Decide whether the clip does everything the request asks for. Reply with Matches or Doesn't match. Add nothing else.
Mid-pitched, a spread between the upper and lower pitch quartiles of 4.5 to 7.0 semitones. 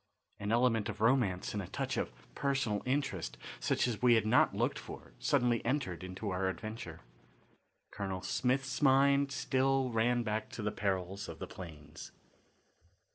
Doesn't match